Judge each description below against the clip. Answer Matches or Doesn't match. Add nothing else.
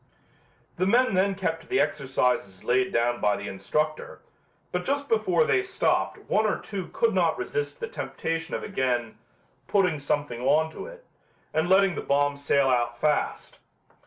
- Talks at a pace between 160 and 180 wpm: Matches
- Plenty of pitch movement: Matches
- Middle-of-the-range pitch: Matches